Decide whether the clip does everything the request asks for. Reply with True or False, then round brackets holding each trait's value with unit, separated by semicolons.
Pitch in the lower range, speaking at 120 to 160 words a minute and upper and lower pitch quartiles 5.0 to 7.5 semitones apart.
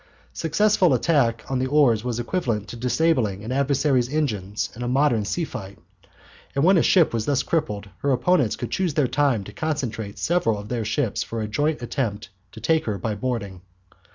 False (125 Hz; 195 wpm; 5.5 semitones)